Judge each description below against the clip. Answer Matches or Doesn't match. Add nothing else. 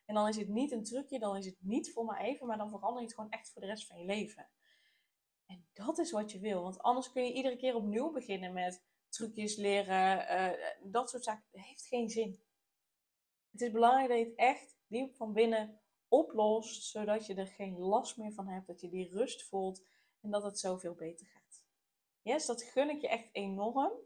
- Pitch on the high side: Matches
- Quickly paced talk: Matches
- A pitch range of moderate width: Matches